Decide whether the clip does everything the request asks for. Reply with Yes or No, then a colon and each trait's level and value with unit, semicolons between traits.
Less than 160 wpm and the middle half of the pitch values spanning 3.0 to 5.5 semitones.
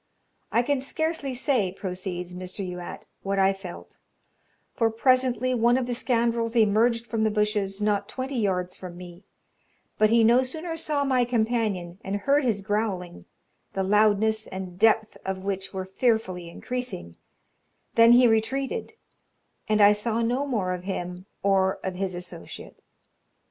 Yes: average, 150 wpm; average, 4.3 semitones